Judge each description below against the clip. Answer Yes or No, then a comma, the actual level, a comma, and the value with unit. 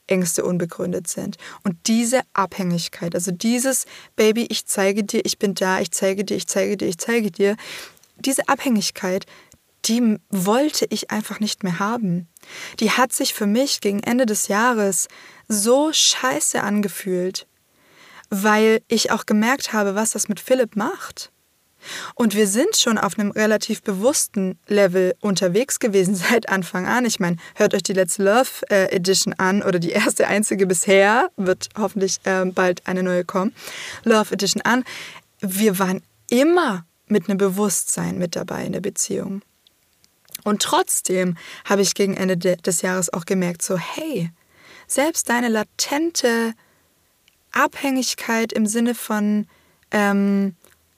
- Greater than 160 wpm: No, average, 145 wpm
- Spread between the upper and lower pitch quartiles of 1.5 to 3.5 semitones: Yes, average, 3.2 semitones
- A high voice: Yes, high, 205 Hz